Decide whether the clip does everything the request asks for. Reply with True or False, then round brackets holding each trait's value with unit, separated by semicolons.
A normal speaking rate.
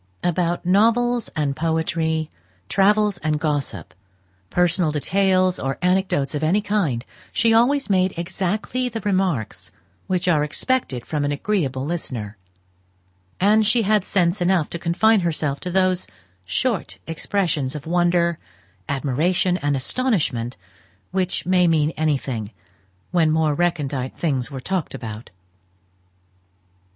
False (120 wpm)